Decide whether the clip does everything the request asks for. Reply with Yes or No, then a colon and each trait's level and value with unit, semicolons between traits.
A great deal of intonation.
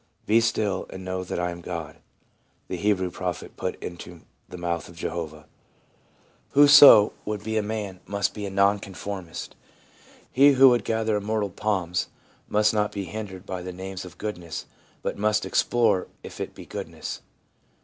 No: average, 3.2 semitones